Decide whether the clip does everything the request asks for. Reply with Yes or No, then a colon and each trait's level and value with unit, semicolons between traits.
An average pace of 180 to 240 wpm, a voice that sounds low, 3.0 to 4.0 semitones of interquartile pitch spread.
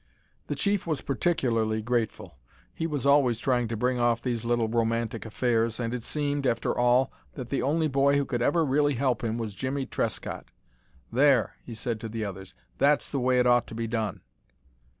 Yes: average, 190 wpm; low, 120 Hz; average, 3.3 semitones